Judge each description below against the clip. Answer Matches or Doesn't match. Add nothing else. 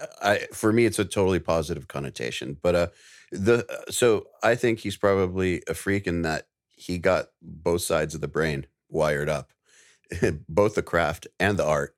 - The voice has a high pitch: Doesn't match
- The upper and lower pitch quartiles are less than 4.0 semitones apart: Doesn't match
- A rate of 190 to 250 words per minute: Doesn't match